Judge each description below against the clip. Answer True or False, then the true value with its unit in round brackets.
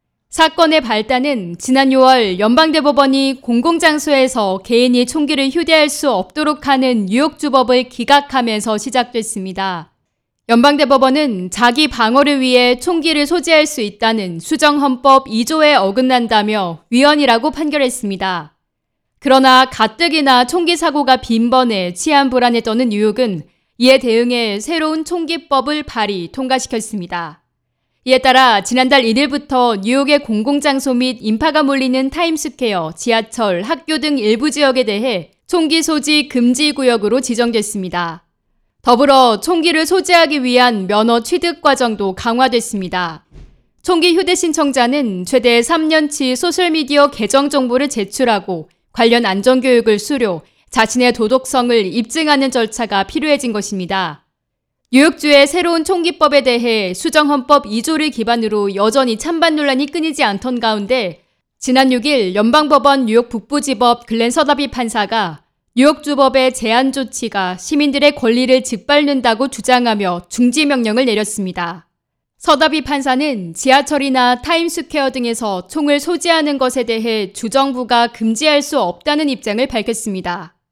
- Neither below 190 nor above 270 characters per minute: False (315 characters per minute)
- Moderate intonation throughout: True (4.7 semitones)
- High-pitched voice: True (255 Hz)